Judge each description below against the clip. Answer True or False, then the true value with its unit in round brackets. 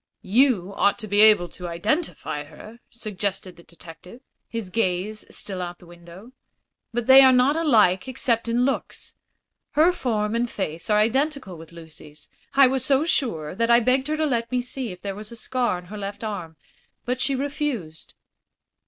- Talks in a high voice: True (215 Hz)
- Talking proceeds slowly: False (185 wpm)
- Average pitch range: False (5.9 semitones)